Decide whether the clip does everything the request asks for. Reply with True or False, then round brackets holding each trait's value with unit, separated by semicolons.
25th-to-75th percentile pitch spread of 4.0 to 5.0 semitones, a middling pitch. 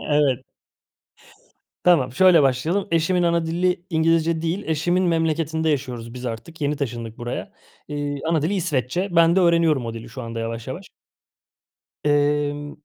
True (4.6 semitones; 155 Hz)